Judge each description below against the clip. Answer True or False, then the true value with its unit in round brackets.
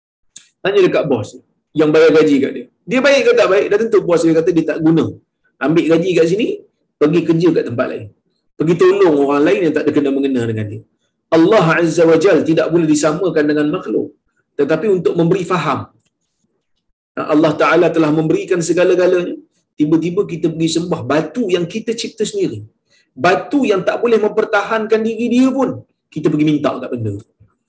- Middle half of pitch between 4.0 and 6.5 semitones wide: True (5.4 semitones)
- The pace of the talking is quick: True (175 wpm)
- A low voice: False (165 Hz)